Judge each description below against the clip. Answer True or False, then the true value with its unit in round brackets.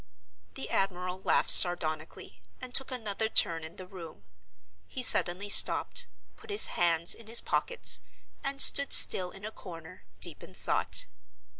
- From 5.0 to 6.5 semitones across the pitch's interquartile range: True (5.3 semitones)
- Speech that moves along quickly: False (150 wpm)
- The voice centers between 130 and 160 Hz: False (190 Hz)